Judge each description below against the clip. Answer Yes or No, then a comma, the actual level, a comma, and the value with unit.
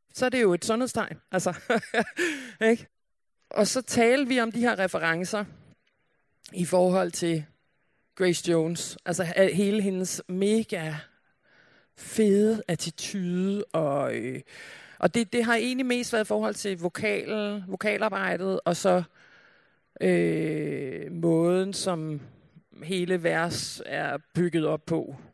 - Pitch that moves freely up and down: No, average, 4.4 semitones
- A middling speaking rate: No, slow, 120 wpm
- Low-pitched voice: No, high, 190 Hz